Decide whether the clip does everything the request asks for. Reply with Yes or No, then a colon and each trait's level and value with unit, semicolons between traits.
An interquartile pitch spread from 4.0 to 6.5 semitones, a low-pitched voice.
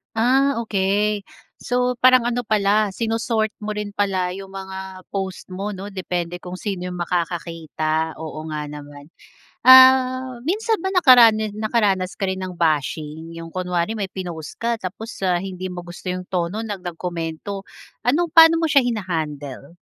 No: average, 4.4 semitones; high, 190 Hz